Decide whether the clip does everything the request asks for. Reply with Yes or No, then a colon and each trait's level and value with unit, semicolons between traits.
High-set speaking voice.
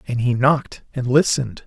No: low, 130 Hz